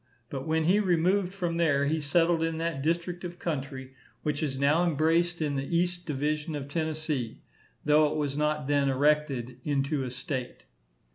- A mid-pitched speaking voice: Yes, medium, 150 Hz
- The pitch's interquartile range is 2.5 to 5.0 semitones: Yes, average, 3.1 semitones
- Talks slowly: No, average, 170 wpm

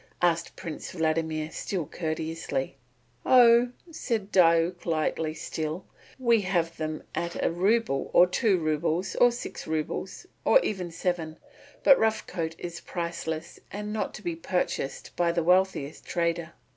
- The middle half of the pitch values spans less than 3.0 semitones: No, average, 3.3 semitones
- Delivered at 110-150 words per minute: Yes, average, 140 wpm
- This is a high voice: No, medium, 170 Hz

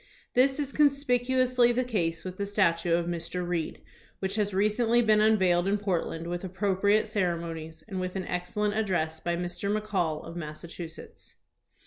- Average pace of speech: Yes, average, 160 wpm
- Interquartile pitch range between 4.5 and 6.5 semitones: No, average, 3.8 semitones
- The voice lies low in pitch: No, high, 190 Hz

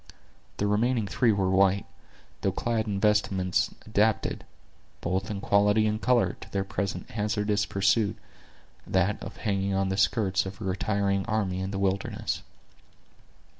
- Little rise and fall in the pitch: Yes, narrow, 1.7 semitones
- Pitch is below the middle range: Yes, low, 100 Hz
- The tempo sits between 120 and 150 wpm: Yes, average, 140 wpm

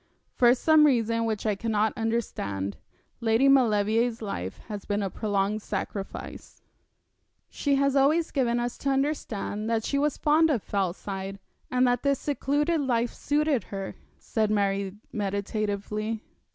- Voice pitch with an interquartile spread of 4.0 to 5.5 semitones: Yes, average, 4.9 semitones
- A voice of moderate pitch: No, high, 225 Hz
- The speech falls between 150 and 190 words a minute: No, average, 140 wpm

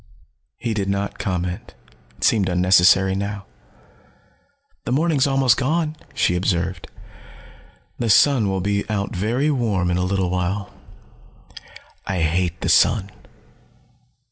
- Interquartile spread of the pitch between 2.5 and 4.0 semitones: No, average, 4.4 semitones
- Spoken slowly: Yes, slow, 120 wpm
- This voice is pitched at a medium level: No, low, 100 Hz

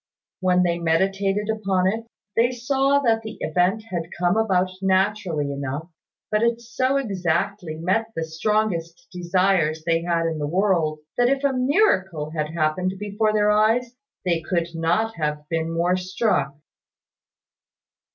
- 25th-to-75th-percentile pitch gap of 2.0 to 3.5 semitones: No, average, 4.6 semitones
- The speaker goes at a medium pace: Yes, average, 145 wpm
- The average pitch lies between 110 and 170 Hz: No, medium, 185 Hz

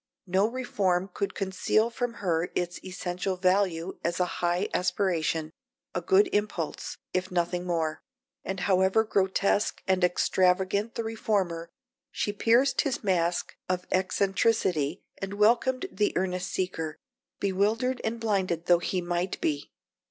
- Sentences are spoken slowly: Yes, slow, 130 wpm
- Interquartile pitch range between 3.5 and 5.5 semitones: No, average, 2.8 semitones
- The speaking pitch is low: No, medium, 185 Hz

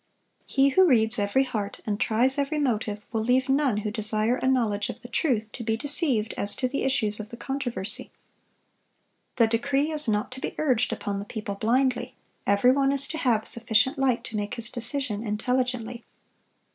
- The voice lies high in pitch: Yes, high, 240 Hz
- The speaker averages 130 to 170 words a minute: No, average, 185 wpm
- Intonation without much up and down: No, average, 3.7 semitones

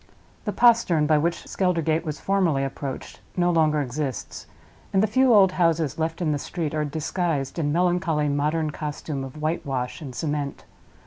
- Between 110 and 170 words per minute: Yes, average, 165 wpm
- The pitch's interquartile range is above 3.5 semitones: No, average, 3.2 semitones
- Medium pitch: Yes, medium, 155 Hz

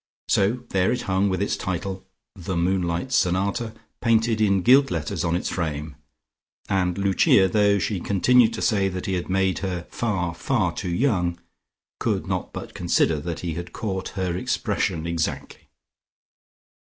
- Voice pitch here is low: Yes, very low, 95 Hz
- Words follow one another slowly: No, average, 155 wpm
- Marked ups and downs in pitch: No, average, 2.8 semitones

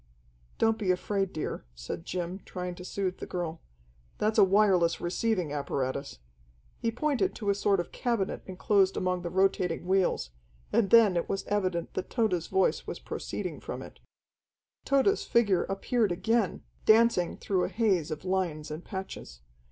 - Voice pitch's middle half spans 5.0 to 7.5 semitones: No, average, 3.4 semitones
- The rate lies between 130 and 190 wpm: Yes, average, 160 wpm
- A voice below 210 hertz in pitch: Yes, high, 190 Hz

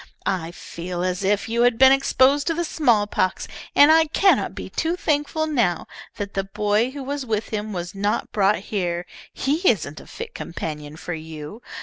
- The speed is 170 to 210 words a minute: Yes, average, 185 wpm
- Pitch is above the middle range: Yes, high, 210 Hz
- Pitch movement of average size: No, wide, 7.4 semitones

